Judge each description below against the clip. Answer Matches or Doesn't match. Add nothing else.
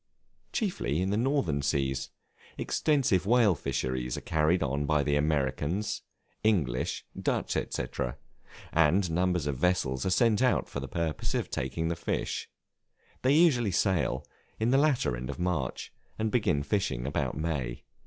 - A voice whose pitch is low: Matches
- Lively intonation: Matches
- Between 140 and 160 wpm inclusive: Matches